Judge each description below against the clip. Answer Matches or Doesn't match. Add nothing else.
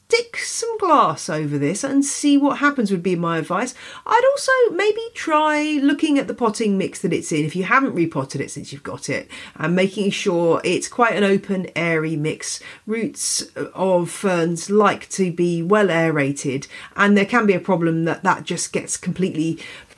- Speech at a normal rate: Matches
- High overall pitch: Matches